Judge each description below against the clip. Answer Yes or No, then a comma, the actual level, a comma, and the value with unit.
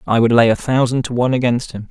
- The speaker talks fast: Yes, fast, 285 wpm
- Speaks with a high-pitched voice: No, low, 120 Hz